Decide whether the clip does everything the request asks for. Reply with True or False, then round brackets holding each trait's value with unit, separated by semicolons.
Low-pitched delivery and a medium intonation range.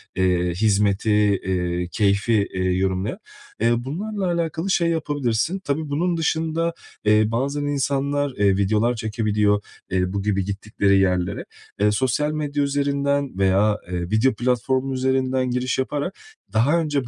False (120 Hz; 6.0 semitones)